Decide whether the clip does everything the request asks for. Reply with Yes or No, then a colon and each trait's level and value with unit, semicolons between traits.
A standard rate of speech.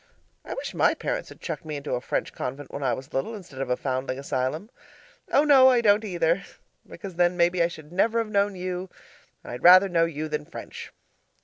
No: fast, 210 wpm